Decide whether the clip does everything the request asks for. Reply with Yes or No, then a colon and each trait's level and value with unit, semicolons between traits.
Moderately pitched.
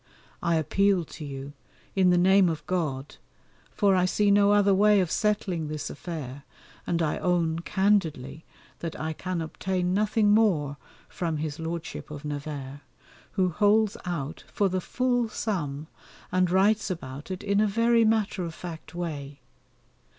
Yes: medium, 180 Hz